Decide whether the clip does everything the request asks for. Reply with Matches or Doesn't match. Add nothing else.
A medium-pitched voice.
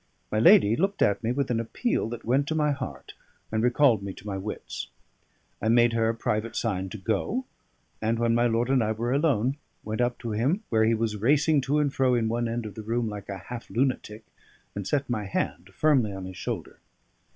Doesn't match